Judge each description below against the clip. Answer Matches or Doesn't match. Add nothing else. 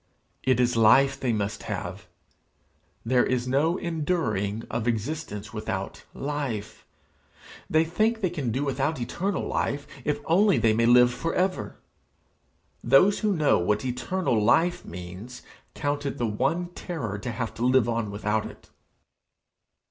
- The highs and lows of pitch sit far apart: Matches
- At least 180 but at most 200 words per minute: Doesn't match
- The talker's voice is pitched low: Matches